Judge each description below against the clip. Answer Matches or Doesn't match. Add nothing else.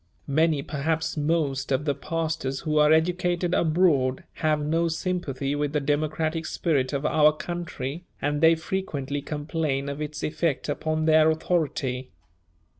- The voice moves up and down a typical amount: Doesn't match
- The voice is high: Doesn't match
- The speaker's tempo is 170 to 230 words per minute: Doesn't match